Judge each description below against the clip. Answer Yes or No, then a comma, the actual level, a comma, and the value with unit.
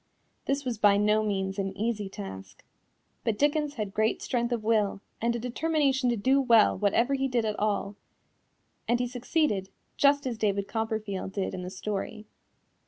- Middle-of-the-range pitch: No, high, 220 Hz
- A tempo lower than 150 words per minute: No, average, 170 wpm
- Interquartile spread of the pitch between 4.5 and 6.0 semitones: No, average, 3.8 semitones